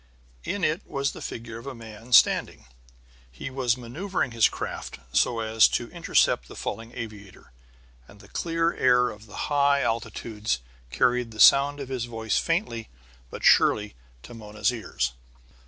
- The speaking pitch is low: Yes, low, 115 Hz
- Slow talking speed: No, average, 155 wpm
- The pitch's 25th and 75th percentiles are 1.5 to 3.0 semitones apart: No, average, 3.8 semitones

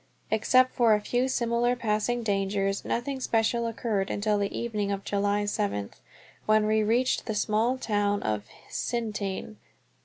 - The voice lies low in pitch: No, high, 215 Hz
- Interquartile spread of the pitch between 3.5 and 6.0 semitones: No, narrow, 2.6 semitones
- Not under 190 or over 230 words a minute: No, average, 145 wpm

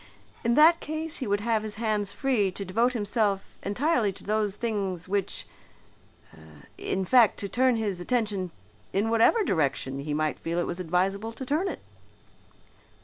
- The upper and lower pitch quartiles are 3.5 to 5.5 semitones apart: Yes, average, 3.9 semitones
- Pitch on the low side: No, high, 210 Hz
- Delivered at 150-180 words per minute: Yes, average, 160 wpm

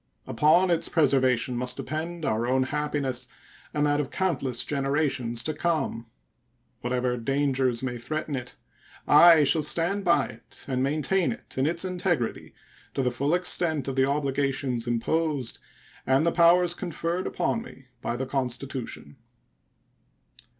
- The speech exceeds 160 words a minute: No, average, 140 wpm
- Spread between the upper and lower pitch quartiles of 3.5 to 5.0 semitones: Yes, average, 4.2 semitones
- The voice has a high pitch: No, medium, 140 Hz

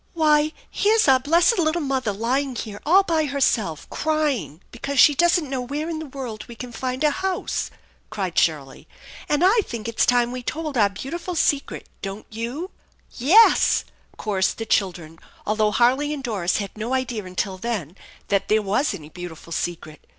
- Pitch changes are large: Yes, wide, 6.7 semitones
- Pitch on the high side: Yes, very high, 250 Hz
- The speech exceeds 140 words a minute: Yes, average, 185 wpm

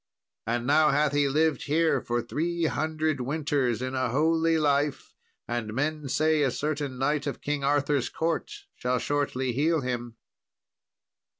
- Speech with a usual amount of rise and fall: Yes, average, 3.2 semitones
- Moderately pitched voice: Yes, medium, 145 Hz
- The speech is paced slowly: No, average, 145 wpm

